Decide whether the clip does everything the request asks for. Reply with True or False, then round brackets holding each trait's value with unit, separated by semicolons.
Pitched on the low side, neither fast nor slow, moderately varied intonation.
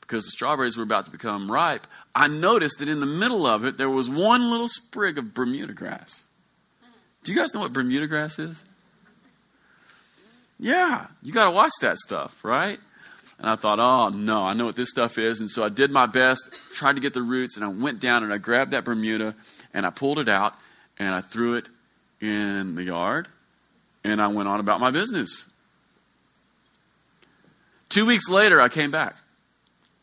False (125 Hz; 190 wpm; 6.2 semitones)